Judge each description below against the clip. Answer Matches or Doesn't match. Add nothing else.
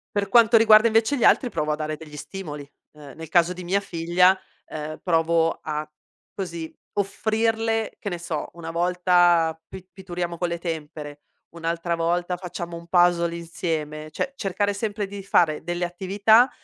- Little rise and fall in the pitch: Doesn't match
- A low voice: Doesn't match